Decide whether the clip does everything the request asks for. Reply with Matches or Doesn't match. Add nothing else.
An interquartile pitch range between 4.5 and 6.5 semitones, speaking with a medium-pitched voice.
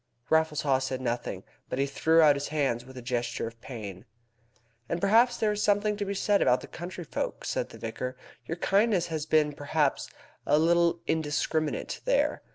Matches